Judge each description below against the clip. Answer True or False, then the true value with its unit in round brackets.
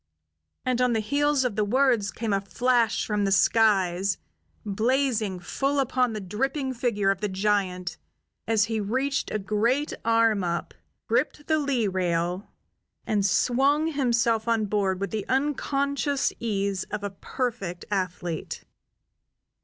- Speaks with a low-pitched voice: False (220 Hz)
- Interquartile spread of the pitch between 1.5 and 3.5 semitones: False (4.6 semitones)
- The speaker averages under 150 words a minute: True (140 wpm)